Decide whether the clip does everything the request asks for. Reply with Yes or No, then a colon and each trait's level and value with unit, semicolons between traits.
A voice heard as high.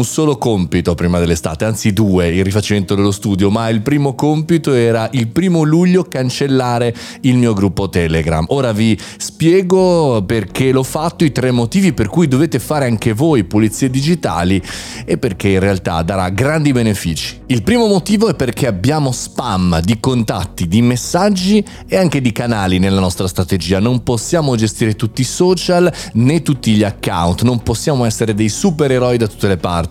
No: low, 120 Hz